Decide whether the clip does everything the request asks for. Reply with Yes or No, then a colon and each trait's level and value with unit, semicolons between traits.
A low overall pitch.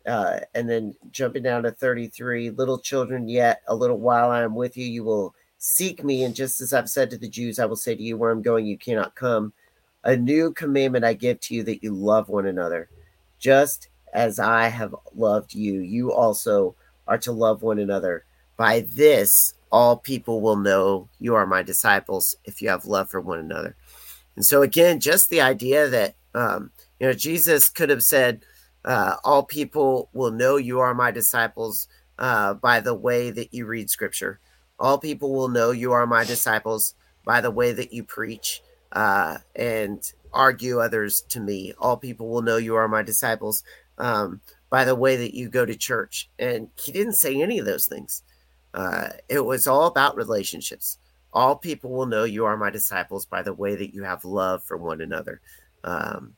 Yes: low, 120 Hz